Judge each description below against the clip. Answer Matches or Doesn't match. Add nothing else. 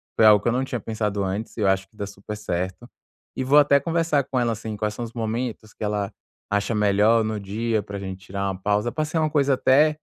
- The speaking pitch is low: Matches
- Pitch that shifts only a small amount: Doesn't match